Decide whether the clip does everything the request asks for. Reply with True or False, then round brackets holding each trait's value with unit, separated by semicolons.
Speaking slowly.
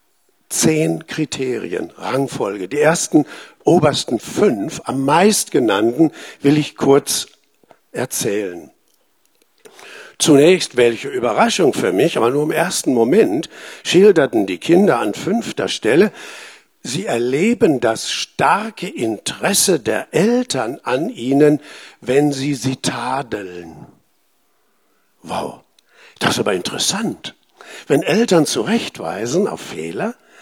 True (105 wpm)